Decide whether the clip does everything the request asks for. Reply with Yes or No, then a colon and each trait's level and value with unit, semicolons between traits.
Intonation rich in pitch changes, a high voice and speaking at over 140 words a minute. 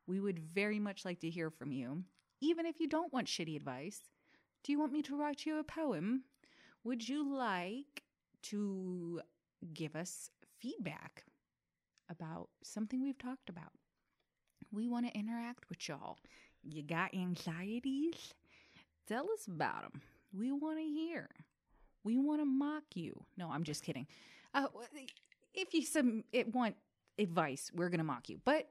Yes: wide, 8.6 semitones; high, 235 Hz; average, 155 wpm